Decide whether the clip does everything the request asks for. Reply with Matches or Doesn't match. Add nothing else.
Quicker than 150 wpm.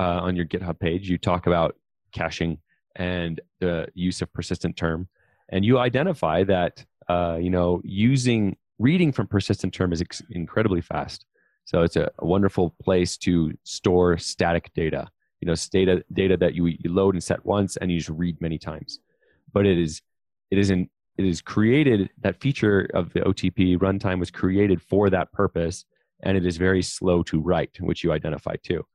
Matches